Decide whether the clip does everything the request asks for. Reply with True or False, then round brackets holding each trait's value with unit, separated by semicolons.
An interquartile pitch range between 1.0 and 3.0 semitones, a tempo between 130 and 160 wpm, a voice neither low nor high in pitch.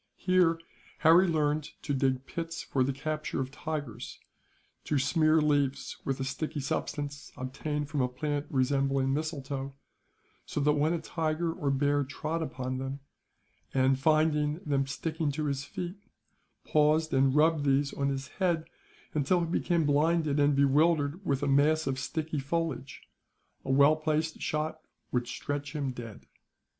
True (2.5 semitones; 150 wpm; 145 Hz)